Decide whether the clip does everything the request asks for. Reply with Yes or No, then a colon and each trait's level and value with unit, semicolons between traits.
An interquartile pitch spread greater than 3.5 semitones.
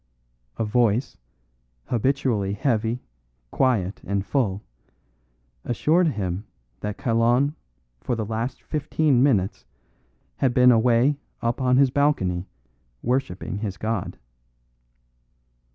Yes: average, 4.3 semitones